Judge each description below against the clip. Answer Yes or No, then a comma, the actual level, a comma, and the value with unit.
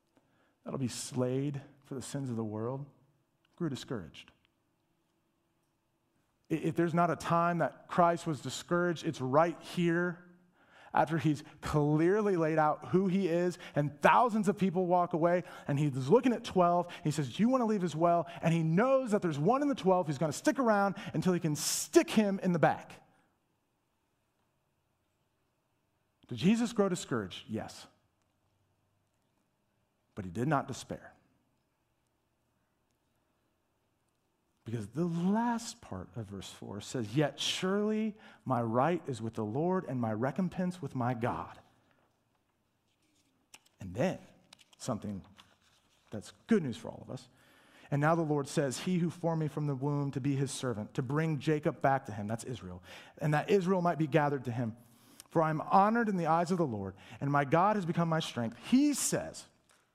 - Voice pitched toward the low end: No, medium, 150 Hz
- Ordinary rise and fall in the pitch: No, wide, 6.3 semitones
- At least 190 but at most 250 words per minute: No, average, 165 wpm